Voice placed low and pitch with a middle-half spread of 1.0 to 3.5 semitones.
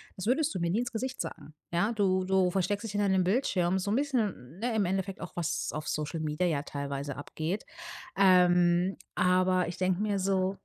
No: medium, 185 Hz; average, 2.9 semitones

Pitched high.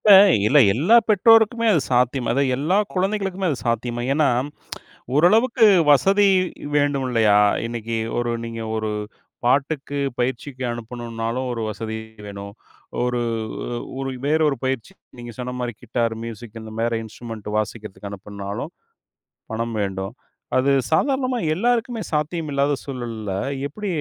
No: low, 125 Hz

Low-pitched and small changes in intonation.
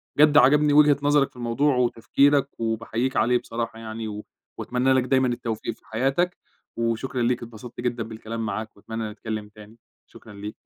No: low, 120 Hz; average, 3.0 semitones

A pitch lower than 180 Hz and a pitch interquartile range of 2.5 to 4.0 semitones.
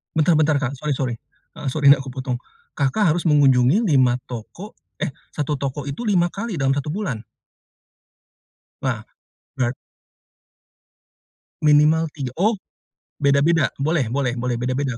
Yes: medium, 140 Hz; average, 3.5 semitones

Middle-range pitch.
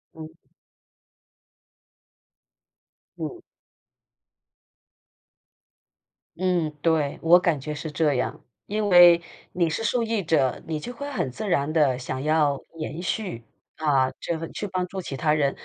Yes: medium, 160 Hz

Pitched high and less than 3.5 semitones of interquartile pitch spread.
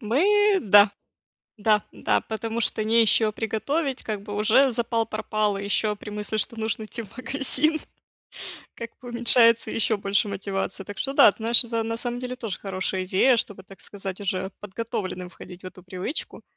Yes: high, 220 Hz; average, 2.7 semitones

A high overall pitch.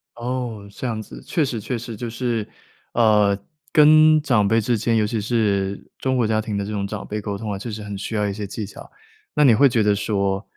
No: low, 110 Hz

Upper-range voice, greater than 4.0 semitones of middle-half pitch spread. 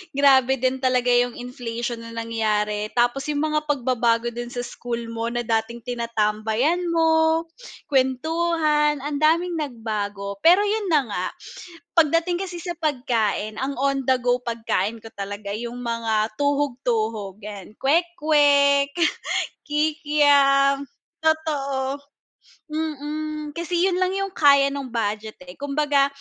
Yes: very high, 270 Hz; average, 4.8 semitones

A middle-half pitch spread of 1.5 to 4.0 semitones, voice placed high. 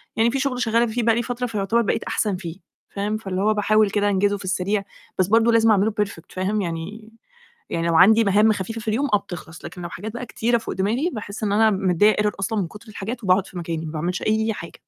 Yes: average, 3.0 semitones; high, 210 Hz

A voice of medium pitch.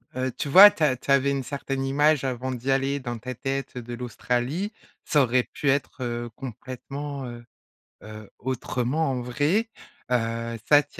No: low, 130 Hz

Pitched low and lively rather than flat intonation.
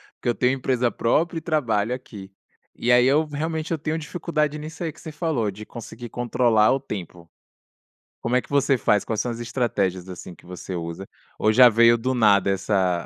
Yes: low, 120 Hz; wide, 5.9 semitones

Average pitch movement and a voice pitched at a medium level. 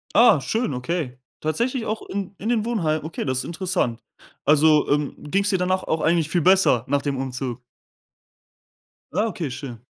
No: wide, 5.9 semitones; medium, 160 Hz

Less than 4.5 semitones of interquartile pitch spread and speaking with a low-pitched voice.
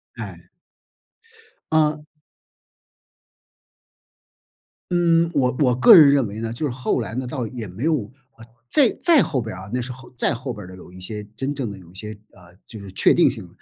No: average, 5.3 semitones; low, 125 Hz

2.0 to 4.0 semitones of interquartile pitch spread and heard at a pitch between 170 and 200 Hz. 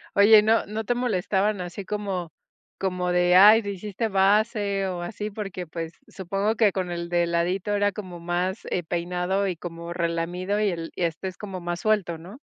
Yes: average, 2.9 semitones; high, 190 Hz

